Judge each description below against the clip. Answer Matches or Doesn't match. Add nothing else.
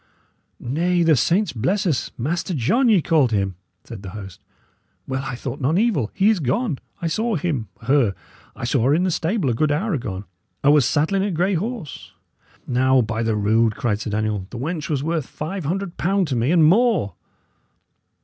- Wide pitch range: Matches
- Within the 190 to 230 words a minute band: Matches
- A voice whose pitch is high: Doesn't match